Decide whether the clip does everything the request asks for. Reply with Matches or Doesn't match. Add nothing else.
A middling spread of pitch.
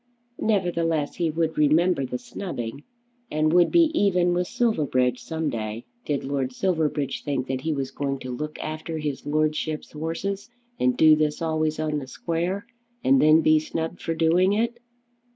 Matches